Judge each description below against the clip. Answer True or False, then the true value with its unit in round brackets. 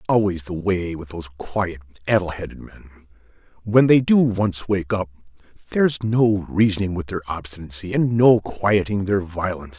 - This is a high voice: False (95 Hz)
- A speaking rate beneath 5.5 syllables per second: False (5.6 syllables/s)